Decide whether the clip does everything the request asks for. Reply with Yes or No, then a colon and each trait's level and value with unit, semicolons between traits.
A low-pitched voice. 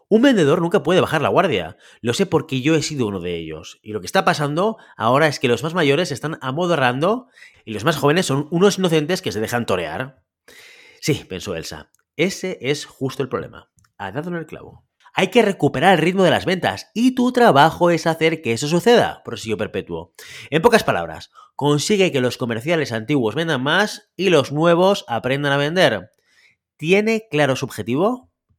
No: medium, 155 Hz